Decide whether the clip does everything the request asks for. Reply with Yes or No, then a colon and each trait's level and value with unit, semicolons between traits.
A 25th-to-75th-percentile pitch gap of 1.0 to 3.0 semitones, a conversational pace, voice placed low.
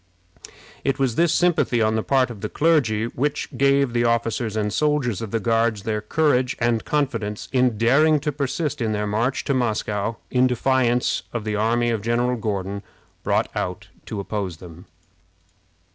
No: average, 3.7 semitones; average, 170 wpm; low, 120 Hz